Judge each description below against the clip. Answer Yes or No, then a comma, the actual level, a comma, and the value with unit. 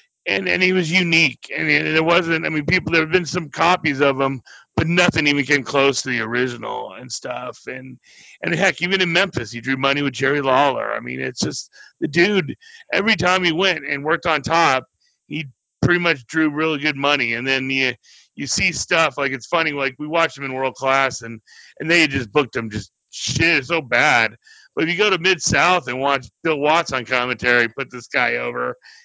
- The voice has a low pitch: No, medium, 145 Hz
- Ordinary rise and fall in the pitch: Yes, average, 4.5 semitones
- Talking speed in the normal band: No, fast, 215 wpm